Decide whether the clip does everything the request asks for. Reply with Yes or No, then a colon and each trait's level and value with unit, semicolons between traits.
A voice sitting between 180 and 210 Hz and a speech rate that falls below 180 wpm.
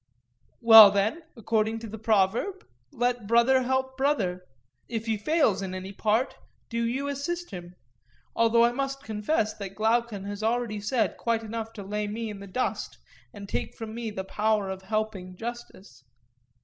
No: high, 220 Hz; average, 160 wpm